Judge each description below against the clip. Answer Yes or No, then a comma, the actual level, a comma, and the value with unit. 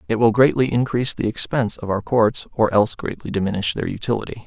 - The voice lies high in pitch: No, low, 110 Hz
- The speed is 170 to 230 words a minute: Yes, average, 200 wpm